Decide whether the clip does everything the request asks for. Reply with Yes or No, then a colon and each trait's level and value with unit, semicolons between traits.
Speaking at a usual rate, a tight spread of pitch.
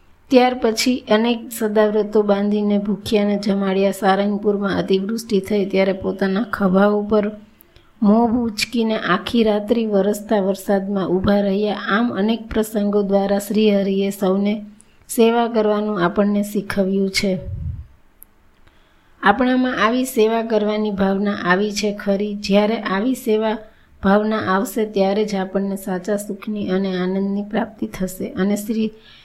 Yes: average, 105 wpm; narrow, 1.7 semitones